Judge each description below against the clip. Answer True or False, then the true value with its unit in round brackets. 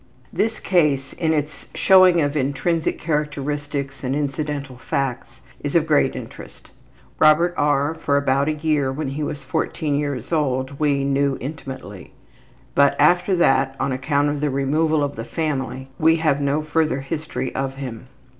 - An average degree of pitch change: False (2.3 semitones)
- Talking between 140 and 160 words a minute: True (155 wpm)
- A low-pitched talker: False (145 Hz)